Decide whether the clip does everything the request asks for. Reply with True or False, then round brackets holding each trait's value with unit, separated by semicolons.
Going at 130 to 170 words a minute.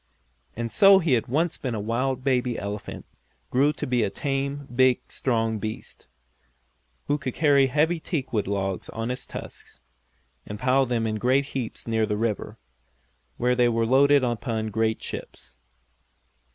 True (160 wpm)